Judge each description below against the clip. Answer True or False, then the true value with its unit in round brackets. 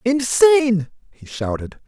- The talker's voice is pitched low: False (180 Hz)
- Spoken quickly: False (95 wpm)